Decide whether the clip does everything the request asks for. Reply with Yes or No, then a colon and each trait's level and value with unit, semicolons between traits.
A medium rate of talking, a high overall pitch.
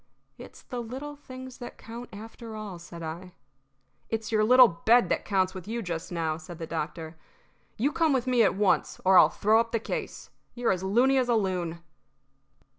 Yes: average, 190 wpm; high, 215 Hz